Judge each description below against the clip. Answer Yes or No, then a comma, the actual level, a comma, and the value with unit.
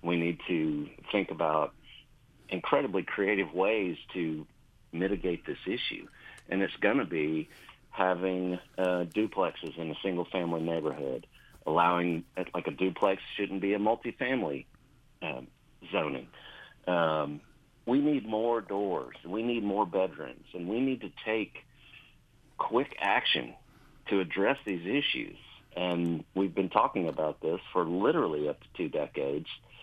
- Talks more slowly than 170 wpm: Yes, slow, 135 wpm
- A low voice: Yes, very low, 90 Hz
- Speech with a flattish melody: No, average, 4.1 semitones